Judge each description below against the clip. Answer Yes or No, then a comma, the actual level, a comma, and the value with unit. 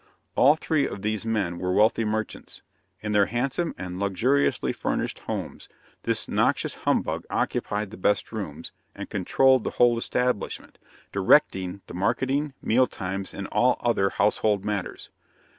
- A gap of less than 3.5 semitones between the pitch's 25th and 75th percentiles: No, average, 4.2 semitones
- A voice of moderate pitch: No, low, 105 Hz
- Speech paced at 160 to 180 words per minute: No, average, 140 wpm